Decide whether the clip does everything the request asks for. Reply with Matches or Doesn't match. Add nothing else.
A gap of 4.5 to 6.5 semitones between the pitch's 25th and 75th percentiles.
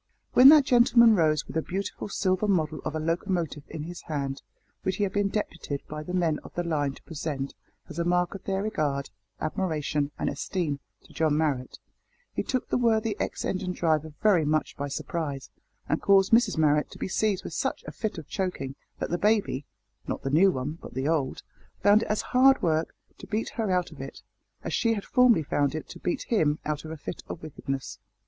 Matches